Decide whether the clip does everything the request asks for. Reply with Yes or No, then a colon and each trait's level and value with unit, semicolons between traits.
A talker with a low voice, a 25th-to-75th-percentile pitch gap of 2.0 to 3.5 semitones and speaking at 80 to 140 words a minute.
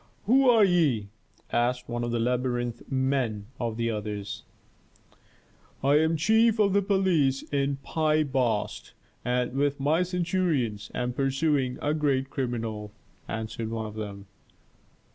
No: low, 130 Hz; average, 5.1 semitones; slow, 135 wpm